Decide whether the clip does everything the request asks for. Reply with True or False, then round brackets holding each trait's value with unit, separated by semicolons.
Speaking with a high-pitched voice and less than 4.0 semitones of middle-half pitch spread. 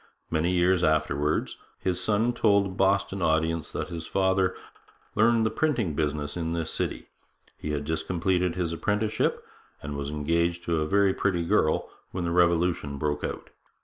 False (85 Hz; 3.5 semitones)